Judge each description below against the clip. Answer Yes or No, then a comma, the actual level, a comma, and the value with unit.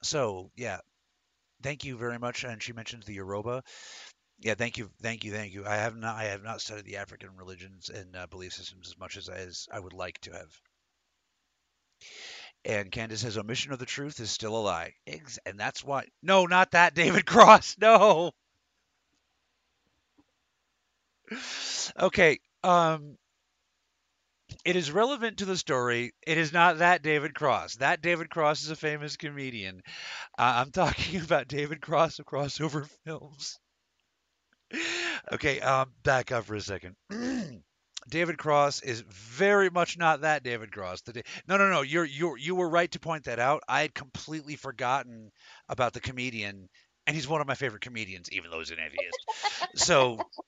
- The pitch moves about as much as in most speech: No, wide, 7.0 semitones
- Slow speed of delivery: No, average, 170 wpm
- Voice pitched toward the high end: No, low, 135 Hz